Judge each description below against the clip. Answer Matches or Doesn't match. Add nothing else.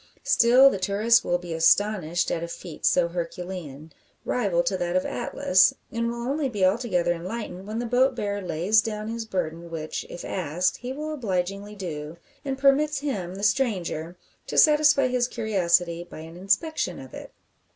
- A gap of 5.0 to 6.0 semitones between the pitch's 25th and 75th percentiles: Matches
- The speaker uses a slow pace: Doesn't match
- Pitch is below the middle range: Doesn't match